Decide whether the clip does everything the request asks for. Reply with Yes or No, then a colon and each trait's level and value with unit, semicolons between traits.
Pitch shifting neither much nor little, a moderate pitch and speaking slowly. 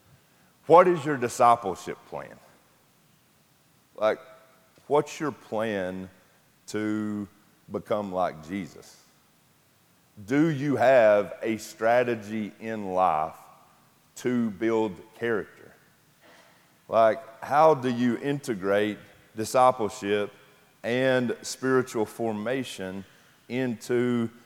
No: average, 3.6 semitones; low, 110 Hz; slow, 80 wpm